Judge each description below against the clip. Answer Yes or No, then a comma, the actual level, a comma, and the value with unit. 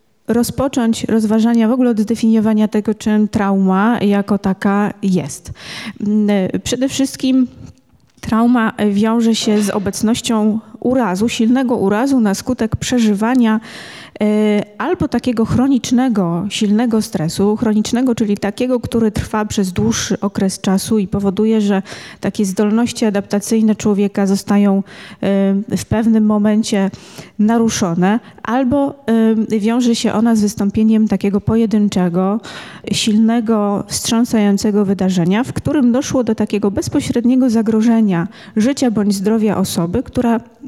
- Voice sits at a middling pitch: No, high, 220 Hz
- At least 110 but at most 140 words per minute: Yes, average, 115 wpm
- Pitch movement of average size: No, narrow, 2.3 semitones